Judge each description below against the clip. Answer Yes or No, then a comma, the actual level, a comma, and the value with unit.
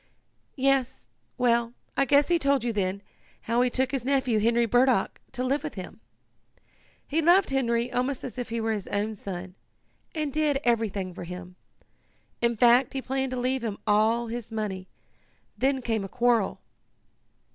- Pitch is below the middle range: No, high, 240 Hz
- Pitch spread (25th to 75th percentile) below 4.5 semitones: Yes, average, 3.4 semitones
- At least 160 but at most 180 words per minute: Yes, average, 170 wpm